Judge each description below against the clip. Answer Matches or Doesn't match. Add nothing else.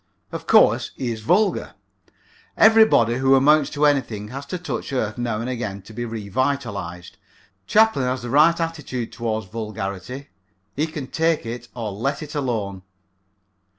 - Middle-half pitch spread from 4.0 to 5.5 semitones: Matches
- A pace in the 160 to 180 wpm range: Doesn't match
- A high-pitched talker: Doesn't match